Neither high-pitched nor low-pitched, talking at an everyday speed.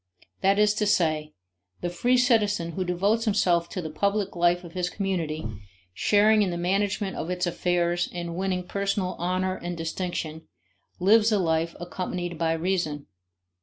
Yes: medium, 180 Hz; average, 160 wpm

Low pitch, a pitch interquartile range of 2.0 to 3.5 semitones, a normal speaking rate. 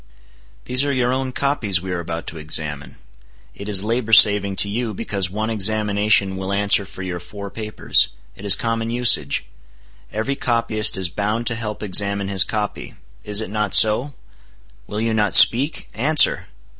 Yes: low, 105 Hz; average, 2.7 semitones; average, 170 wpm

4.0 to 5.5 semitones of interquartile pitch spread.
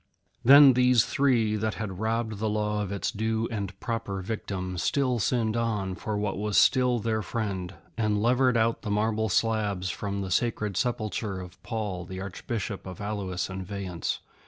No: average, 2.8 semitones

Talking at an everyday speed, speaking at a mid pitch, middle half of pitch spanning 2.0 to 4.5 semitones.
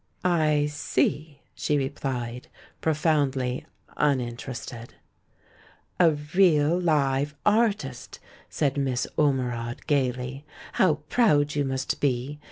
No: slow, 90 wpm; medium, 145 Hz; average, 2.9 semitones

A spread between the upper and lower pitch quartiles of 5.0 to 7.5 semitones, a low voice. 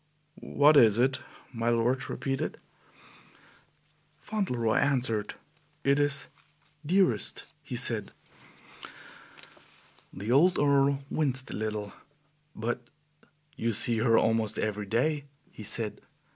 No: average, 4.1 semitones; low, 120 Hz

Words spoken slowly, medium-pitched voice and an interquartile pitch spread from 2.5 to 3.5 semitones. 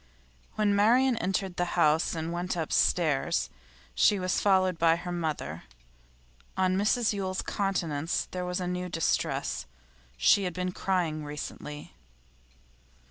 Yes: slow, 130 wpm; medium, 180 Hz; average, 2.8 semitones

